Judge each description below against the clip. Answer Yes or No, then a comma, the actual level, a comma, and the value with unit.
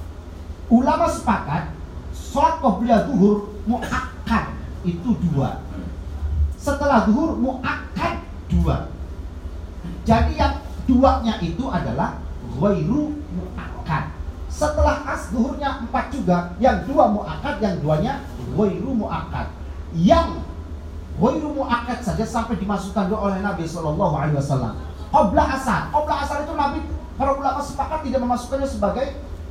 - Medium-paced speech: Yes, average, 105 wpm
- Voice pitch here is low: No, high, 200 Hz